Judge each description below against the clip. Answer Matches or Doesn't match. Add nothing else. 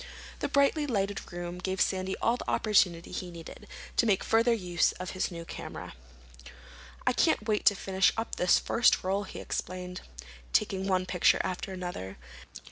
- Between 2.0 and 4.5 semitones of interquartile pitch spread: Matches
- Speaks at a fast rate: Doesn't match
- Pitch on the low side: Doesn't match